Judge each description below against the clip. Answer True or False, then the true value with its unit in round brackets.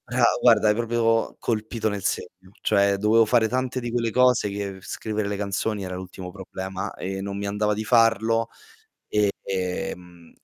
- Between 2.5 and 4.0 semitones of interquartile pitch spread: True (2.9 semitones)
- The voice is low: True (105 Hz)